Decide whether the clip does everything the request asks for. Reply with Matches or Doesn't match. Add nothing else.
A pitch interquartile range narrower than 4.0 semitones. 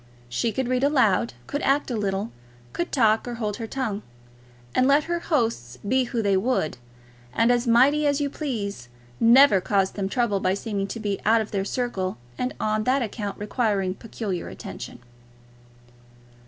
Doesn't match